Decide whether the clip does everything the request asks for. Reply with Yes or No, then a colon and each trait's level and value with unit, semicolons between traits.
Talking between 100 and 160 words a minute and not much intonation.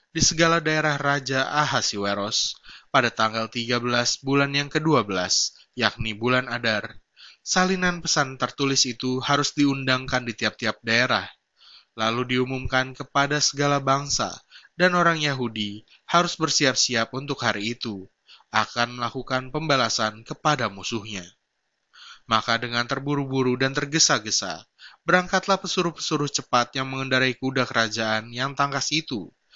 No: average, 115 wpm; average, 3.9 semitones